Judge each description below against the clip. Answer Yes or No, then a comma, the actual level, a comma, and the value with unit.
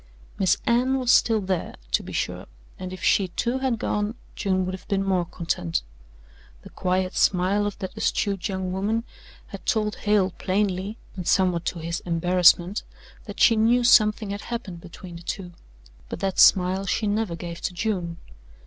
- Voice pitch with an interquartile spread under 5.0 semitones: Yes, average, 2.7 semitones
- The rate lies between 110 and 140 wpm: No, average, 175 wpm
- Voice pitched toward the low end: No, high, 190 Hz